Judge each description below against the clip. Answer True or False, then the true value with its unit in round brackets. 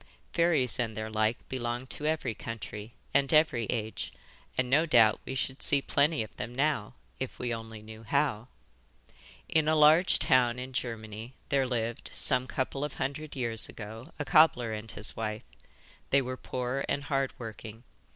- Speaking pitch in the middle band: False (125 Hz)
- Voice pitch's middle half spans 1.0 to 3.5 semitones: False (4.0 semitones)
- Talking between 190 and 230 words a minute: False (170 wpm)